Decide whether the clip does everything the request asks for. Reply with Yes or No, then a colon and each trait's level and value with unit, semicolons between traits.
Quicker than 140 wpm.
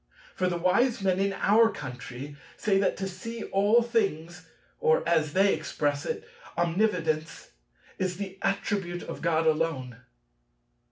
No: slow, 135 wpm